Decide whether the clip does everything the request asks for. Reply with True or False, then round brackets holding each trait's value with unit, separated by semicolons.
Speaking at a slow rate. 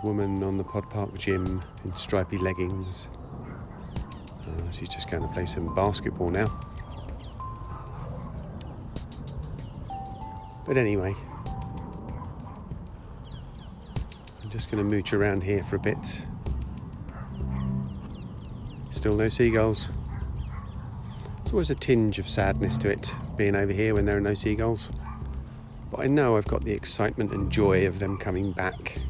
True (130 wpm)